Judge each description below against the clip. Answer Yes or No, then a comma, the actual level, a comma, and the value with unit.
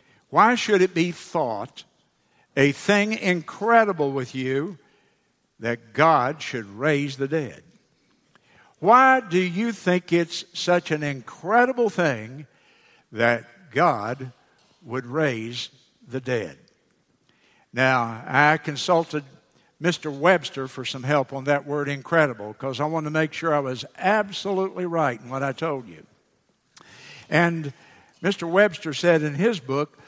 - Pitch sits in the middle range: Yes, medium, 150 Hz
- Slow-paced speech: Yes, slow, 130 wpm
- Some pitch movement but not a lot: Yes, average, 5.0 semitones